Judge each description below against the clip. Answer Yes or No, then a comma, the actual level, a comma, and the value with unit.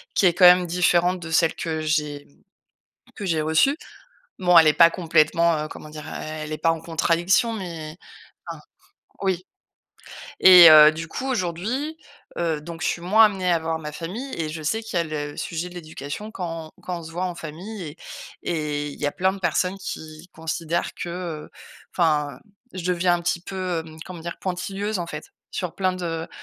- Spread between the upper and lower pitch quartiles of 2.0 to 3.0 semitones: Yes, narrow, 2.6 semitones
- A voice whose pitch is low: No, medium, 170 Hz